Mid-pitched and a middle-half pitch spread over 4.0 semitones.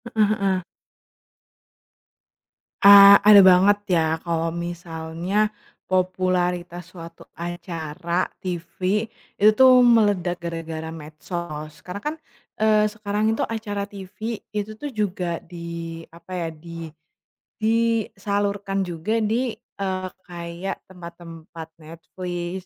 No: medium, 180 Hz; average, 3.2 semitones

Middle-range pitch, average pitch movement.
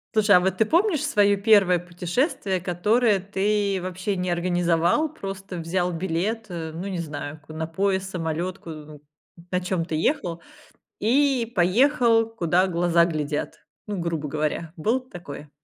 Yes: medium, 180 Hz; average, 3.7 semitones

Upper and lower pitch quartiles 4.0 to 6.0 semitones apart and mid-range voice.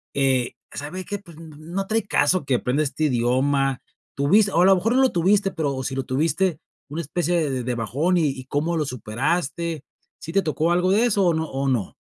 Yes: average, 5.0 semitones; medium, 155 Hz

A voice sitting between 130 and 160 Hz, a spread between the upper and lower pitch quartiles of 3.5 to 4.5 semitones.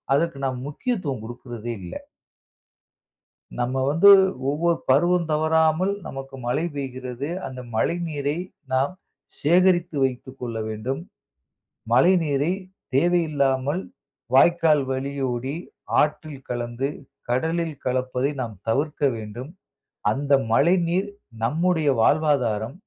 Yes: medium, 140 Hz; average, 4.1 semitones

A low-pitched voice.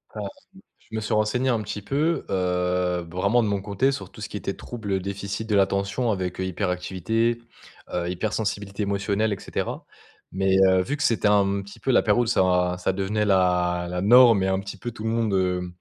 Yes: low, 100 Hz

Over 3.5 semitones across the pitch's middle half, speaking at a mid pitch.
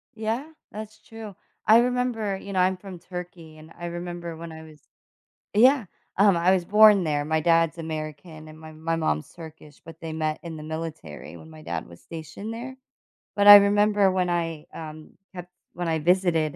Yes: average, 4.2 semitones; medium, 170 Hz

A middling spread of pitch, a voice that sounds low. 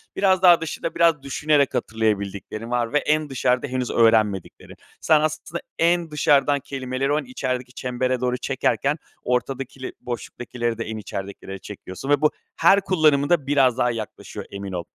Yes: average, 4.4 semitones; low, 130 Hz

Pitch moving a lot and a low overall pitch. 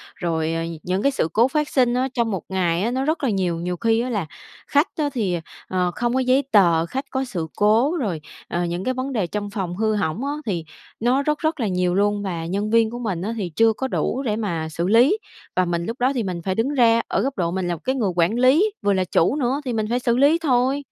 No: wide, 6.1 semitones; high, 220 Hz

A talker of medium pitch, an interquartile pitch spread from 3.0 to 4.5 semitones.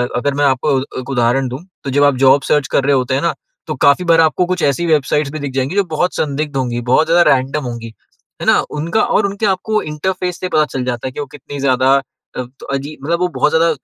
Yes: medium, 145 Hz; average, 4.0 semitones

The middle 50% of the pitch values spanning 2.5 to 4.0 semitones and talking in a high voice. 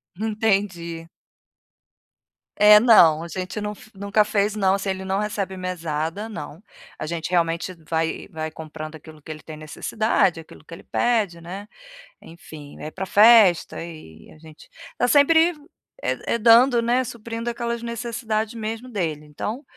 No: average, 5.3 semitones; high, 195 Hz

